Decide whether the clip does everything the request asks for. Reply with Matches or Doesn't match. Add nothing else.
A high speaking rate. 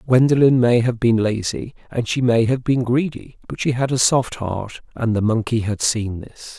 Matches